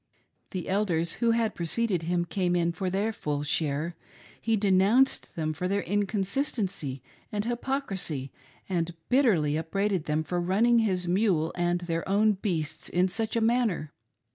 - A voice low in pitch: No, medium, 185 Hz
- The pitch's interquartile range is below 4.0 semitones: No, average, 4.3 semitones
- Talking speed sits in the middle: Yes, average, 150 wpm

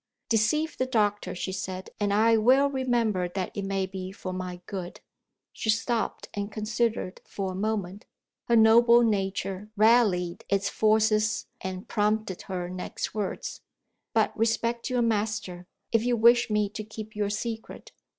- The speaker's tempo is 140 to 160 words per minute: Yes, average, 150 wpm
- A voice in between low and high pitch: No, high, 215 Hz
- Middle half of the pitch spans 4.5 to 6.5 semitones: No, average, 3.0 semitones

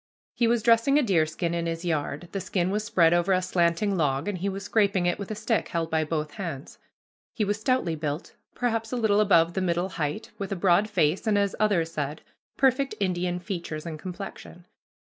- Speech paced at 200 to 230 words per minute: Yes, fast, 205 wpm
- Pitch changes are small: No, average, 4.0 semitones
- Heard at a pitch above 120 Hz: Yes, medium, 185 Hz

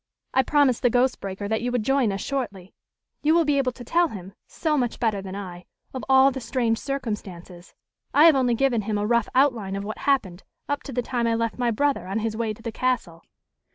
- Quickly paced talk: Yes, fast, 230 wpm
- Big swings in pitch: No, average, 4.5 semitones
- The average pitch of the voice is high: Yes, high, 235 Hz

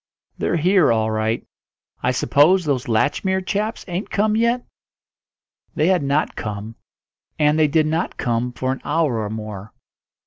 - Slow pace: No, average, 150 wpm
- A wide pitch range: Yes, wide, 7.9 semitones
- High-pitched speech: No, medium, 150 Hz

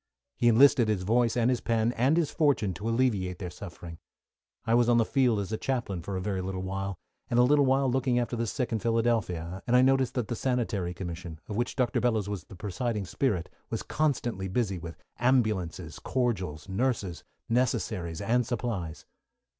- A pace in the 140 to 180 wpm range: No, average, 190 wpm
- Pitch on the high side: No, low, 115 Hz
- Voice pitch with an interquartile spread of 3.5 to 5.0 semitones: Yes, average, 4.7 semitones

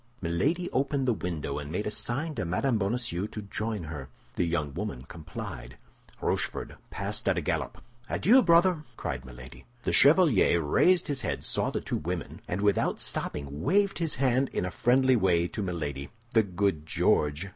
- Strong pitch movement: Yes, wide, 8.9 semitones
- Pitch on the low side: Yes, low, 100 Hz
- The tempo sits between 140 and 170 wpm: No, average, 180 wpm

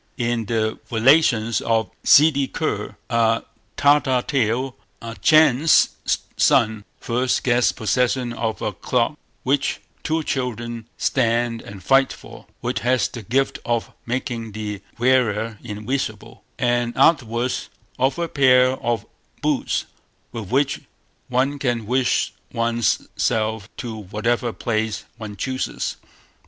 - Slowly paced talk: Yes, slow, 120 wpm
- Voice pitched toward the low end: Yes, low, 120 Hz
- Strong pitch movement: No, average, 2.7 semitones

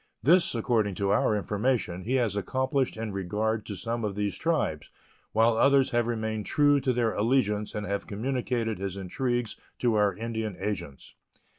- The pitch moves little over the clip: No, average, 3.3 semitones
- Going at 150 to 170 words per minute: Yes, average, 165 wpm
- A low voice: Yes, low, 110 Hz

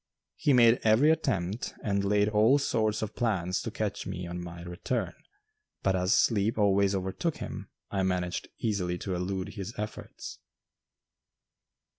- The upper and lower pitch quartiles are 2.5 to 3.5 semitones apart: Yes, average, 3.2 semitones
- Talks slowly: No, average, 145 wpm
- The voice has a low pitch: Yes, low, 100 Hz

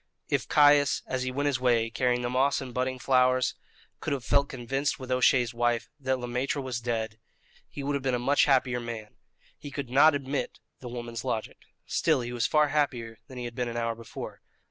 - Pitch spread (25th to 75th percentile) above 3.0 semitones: No, narrow, 2.4 semitones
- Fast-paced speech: Yes, fast, 210 wpm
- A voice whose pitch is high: No, low, 125 Hz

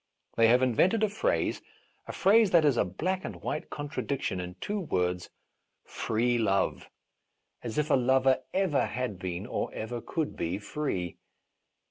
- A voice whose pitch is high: No, low, 125 Hz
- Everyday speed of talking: Yes, average, 170 wpm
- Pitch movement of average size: No, wide, 8.0 semitones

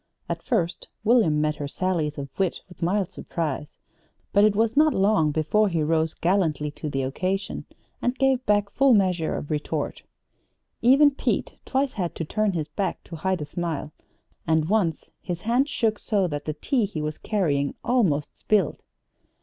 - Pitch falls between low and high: Yes, medium, 180 Hz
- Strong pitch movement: Yes, wide, 5.8 semitones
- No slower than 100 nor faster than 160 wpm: No, average, 175 wpm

